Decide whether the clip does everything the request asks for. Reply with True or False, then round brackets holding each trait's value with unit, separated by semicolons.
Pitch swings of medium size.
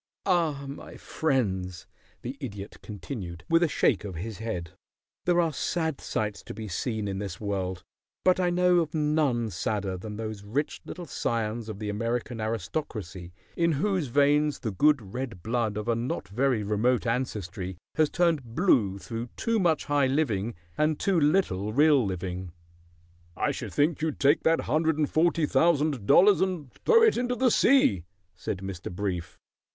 False (7.5 semitones)